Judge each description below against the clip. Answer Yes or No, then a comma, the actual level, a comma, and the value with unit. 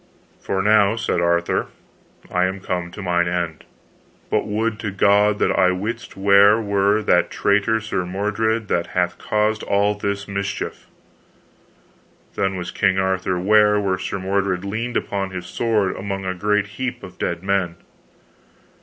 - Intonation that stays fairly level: Yes, narrow, 2.1 semitones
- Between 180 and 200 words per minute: No, average, 155 wpm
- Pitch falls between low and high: No, low, 100 Hz